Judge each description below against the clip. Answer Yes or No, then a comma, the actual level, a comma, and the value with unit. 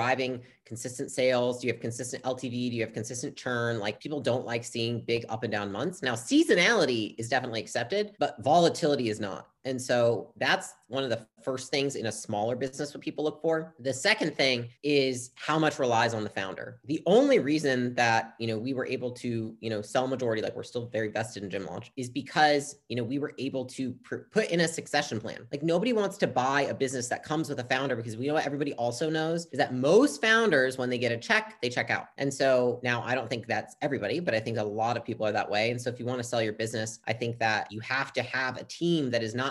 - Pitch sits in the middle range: No, low, 130 Hz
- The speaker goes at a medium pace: No, fast, 250 wpm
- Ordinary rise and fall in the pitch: Yes, average, 3.6 semitones